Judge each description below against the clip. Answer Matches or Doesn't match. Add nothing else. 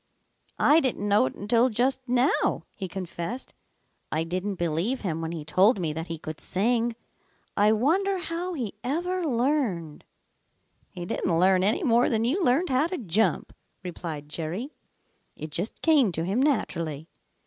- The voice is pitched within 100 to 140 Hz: Doesn't match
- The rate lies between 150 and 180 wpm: Matches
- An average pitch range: Doesn't match